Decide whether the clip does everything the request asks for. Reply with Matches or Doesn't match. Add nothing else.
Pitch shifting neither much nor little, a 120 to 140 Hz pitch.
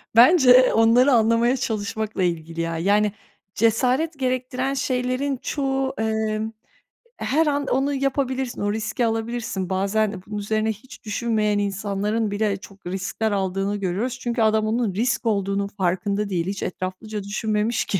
Doesn't match